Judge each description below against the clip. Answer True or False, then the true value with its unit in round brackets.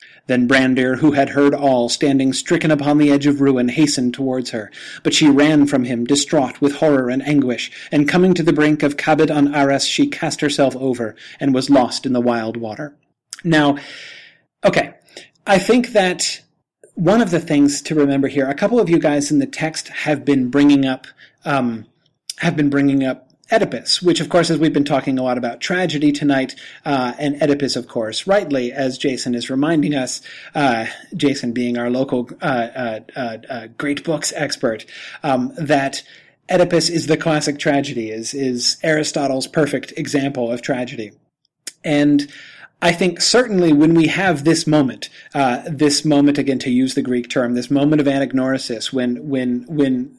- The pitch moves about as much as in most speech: True (3.0 semitones)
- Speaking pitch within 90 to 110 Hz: False (140 Hz)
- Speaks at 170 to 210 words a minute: True (180 wpm)